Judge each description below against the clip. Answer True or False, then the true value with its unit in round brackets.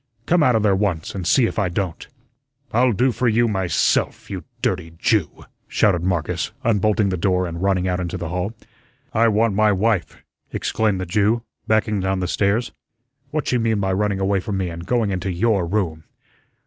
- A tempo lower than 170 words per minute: False (185 wpm)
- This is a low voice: True (100 Hz)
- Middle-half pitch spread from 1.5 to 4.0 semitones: True (3.3 semitones)